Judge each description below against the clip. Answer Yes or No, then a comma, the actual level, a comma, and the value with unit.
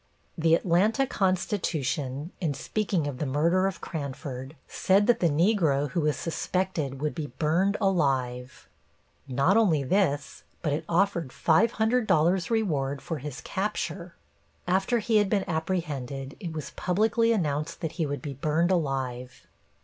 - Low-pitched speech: No, medium, 165 Hz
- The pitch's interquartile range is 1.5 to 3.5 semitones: No, average, 5.2 semitones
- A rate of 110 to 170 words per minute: Yes, average, 140 wpm